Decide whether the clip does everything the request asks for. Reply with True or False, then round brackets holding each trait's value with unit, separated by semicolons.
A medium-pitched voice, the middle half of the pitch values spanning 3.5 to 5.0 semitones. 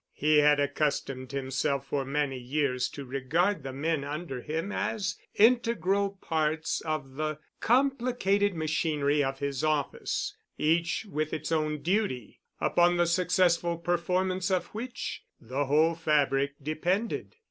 True (155 Hz; 4.3 semitones)